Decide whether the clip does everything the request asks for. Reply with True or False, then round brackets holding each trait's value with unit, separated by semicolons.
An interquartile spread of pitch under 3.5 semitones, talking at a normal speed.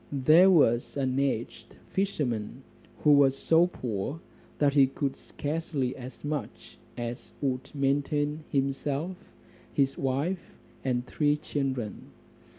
False (2.5 semitones; 115 wpm)